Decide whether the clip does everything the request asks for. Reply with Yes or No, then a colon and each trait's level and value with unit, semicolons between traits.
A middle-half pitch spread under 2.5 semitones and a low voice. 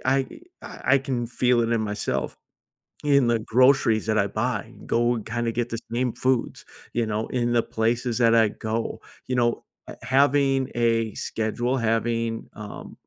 Yes: narrow, 1.8 semitones; low, 120 Hz